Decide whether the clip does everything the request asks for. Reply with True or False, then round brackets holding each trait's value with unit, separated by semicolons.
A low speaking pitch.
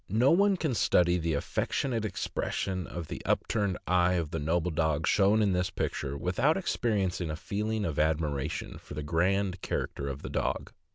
True (90 Hz)